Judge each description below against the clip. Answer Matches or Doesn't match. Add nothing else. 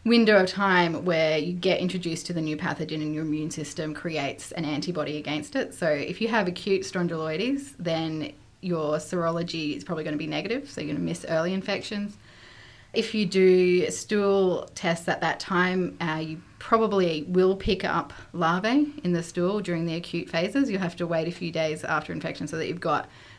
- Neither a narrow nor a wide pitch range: Matches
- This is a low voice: Doesn't match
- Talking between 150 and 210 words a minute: Matches